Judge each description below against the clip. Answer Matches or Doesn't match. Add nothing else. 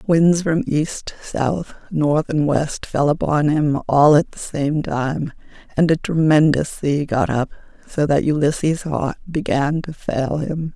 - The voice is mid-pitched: Matches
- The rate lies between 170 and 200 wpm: Doesn't match